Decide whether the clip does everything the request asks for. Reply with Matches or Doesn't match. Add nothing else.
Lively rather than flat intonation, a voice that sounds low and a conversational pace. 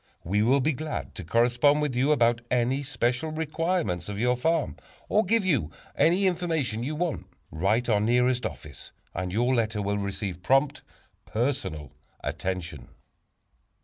Matches